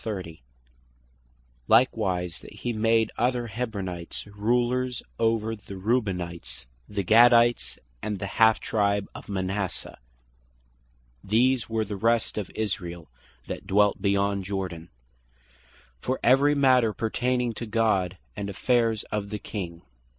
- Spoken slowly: Yes, slow, 115 wpm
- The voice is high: No, low, 105 Hz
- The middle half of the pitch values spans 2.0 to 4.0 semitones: Yes, average, 3.4 semitones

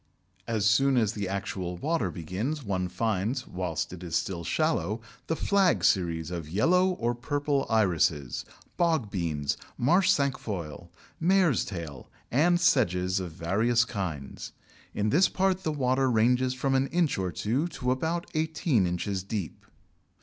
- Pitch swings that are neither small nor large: No, wide, 8.1 semitones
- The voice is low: Yes, low, 110 Hz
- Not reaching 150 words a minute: Yes, average, 140 wpm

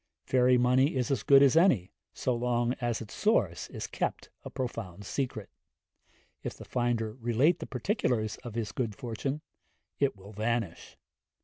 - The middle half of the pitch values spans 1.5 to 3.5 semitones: Yes, average, 3.1 semitones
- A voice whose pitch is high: No, low, 120 Hz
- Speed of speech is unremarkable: Yes, average, 155 wpm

